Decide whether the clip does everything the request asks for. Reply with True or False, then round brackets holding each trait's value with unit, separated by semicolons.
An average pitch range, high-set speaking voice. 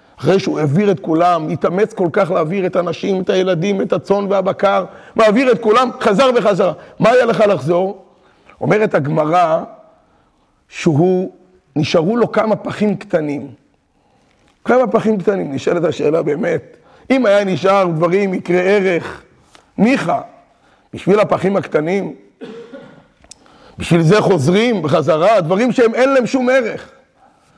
True (3.5 semitones; 195 Hz)